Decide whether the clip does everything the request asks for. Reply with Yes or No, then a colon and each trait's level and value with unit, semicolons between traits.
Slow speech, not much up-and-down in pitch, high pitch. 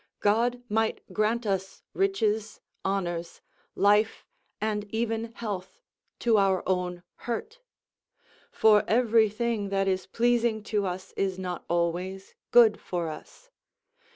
No: slow, 120 wpm; average, 3.1 semitones; high, 210 Hz